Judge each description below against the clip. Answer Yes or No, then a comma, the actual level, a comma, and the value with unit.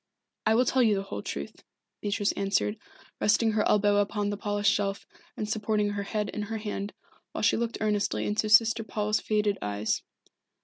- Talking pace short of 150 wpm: No, average, 180 wpm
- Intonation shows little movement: Yes, narrow, 1.1 semitones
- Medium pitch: No, high, 210 Hz